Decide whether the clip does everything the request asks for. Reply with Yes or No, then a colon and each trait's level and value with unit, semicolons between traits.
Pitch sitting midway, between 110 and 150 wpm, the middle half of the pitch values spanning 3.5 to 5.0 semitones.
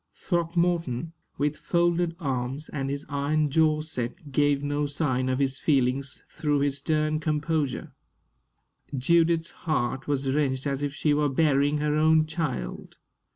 No: medium, 145 Hz; average, 140 wpm; narrow, 2.4 semitones